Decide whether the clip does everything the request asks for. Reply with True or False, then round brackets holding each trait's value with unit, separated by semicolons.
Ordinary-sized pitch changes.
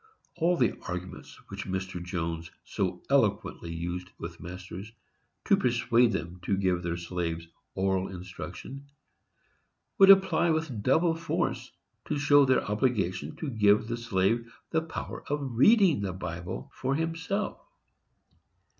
False (7.6 semitones)